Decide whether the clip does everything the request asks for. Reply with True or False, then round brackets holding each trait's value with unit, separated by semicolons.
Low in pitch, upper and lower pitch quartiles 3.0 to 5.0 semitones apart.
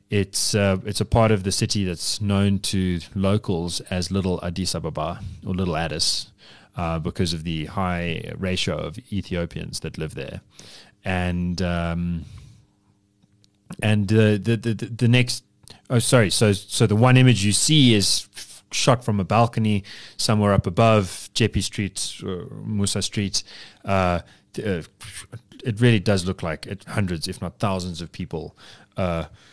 True (100 Hz; 3.3 semitones)